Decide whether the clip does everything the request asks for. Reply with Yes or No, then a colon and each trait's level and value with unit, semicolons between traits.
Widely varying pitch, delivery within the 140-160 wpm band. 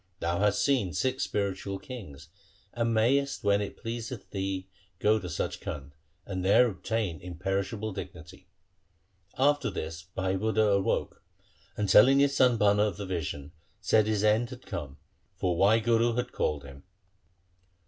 No: average, 4.1 semitones; average, 150 wpm